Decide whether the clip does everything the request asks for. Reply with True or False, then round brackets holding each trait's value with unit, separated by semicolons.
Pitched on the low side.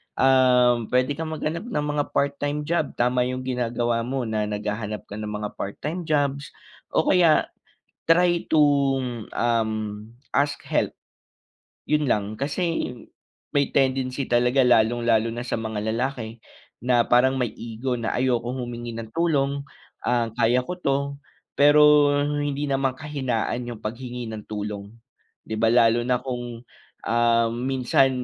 True (125 Hz)